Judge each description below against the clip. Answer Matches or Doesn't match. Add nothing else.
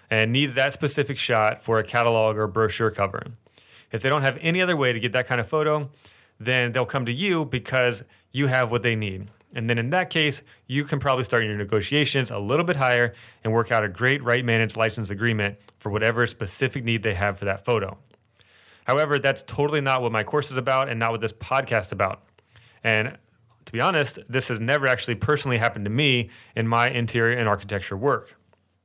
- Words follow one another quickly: Matches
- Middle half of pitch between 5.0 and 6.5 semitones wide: Doesn't match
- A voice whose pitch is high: Doesn't match